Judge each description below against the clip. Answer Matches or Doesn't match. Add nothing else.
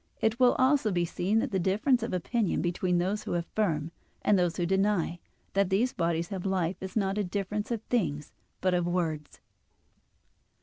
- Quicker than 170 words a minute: Matches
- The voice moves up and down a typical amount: Matches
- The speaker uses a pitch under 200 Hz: Matches